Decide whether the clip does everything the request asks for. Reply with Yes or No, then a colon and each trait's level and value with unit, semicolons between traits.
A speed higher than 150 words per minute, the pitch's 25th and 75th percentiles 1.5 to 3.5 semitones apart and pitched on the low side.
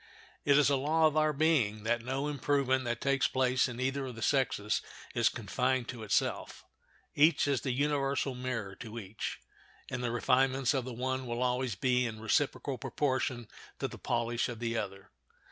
Yes: average, 180 wpm; narrow, 2.6 semitones; low, 130 Hz